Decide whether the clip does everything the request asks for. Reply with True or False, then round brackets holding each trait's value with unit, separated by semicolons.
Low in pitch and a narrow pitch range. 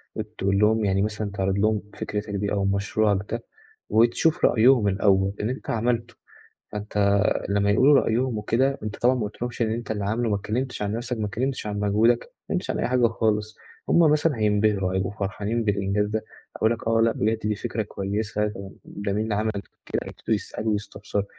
True (105 Hz; 2.1 semitones)